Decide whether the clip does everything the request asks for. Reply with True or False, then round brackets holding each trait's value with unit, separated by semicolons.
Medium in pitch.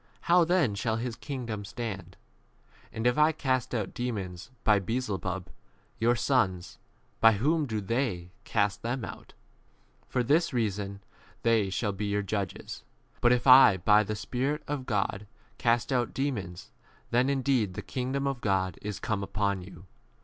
False (110 Hz)